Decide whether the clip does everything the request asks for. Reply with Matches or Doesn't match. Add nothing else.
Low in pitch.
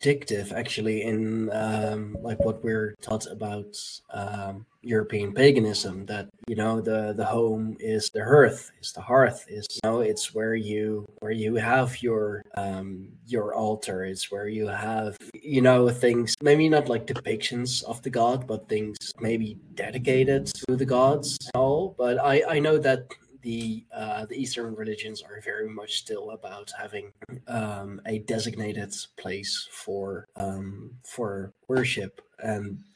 Matches